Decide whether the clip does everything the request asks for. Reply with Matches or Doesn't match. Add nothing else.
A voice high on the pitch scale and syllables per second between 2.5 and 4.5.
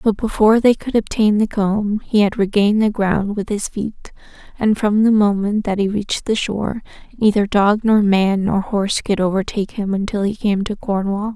Doesn't match